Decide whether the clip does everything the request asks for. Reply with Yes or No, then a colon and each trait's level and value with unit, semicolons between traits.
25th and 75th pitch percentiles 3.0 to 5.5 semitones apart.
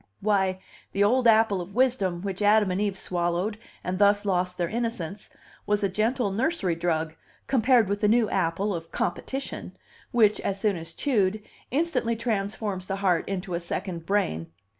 Yes: average, 3.4 semitones